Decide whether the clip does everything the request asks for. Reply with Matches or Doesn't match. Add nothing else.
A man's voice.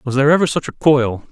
Matches